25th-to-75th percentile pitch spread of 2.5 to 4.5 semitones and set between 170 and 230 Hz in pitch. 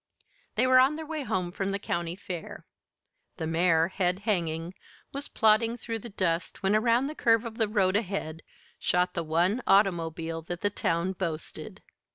No: average, 4.9 semitones; high, 190 Hz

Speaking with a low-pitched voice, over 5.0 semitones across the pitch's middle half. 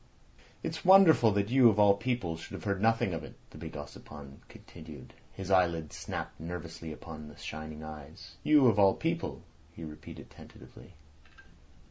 Yes: very low, 85 Hz; wide, 5.5 semitones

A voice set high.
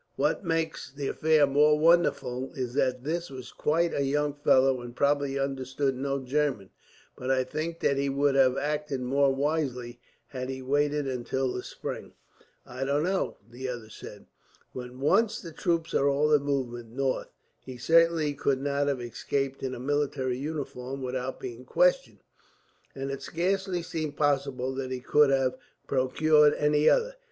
No: medium, 140 Hz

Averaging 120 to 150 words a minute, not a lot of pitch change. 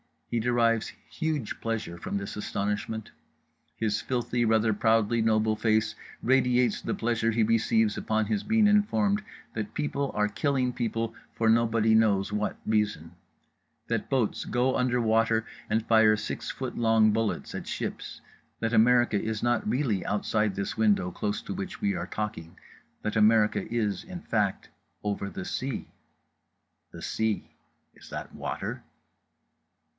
Yes: average, 140 wpm; narrow, 2.3 semitones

